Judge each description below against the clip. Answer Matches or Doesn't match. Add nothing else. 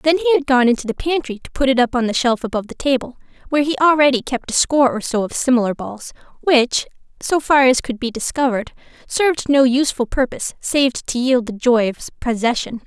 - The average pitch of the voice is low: Doesn't match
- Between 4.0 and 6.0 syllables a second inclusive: Doesn't match